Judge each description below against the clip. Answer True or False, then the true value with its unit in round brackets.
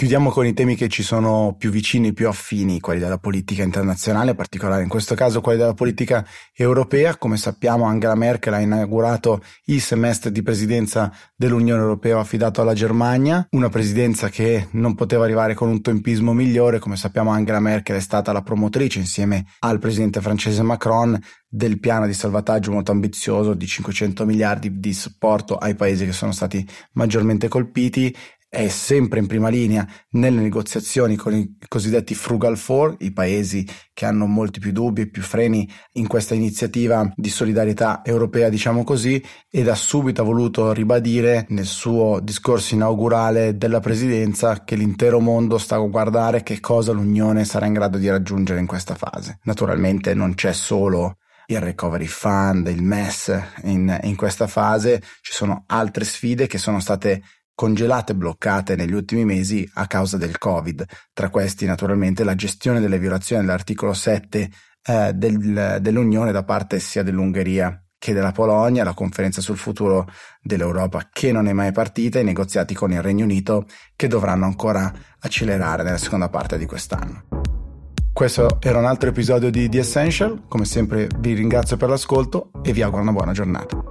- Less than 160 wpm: False (165 wpm)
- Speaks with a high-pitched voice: False (110 Hz)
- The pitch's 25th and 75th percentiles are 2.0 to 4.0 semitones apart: True (2.8 semitones)